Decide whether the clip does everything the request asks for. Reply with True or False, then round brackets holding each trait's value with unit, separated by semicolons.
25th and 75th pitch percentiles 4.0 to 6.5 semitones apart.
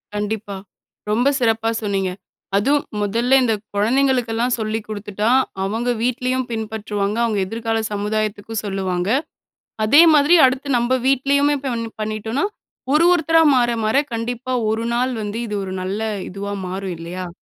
False (3.5 semitones)